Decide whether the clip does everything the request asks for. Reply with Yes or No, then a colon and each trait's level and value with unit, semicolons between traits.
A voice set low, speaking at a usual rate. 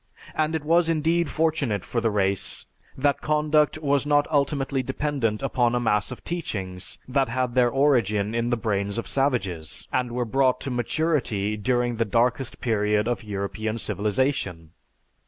Yes: low, 120 Hz; average, 155 wpm